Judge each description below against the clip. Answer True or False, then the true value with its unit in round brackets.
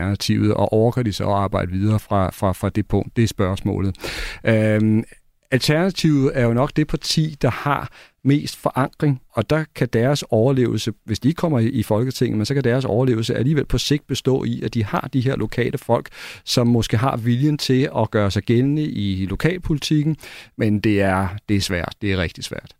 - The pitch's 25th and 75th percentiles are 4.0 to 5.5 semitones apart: True (4.6 semitones)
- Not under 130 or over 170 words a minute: False (200 wpm)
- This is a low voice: True (120 Hz)